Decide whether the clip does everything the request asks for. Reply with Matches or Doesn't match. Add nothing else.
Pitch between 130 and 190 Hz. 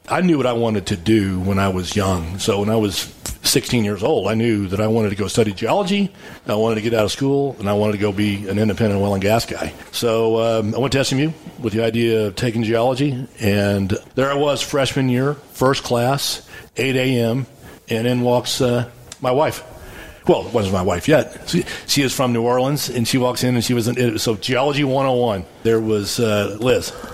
Doesn't match